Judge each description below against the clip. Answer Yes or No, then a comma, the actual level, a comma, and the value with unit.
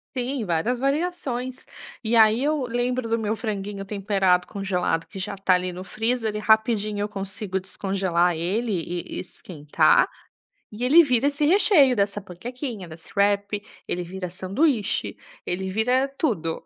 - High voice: Yes, high, 210 Hz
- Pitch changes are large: No, average, 4.7 semitones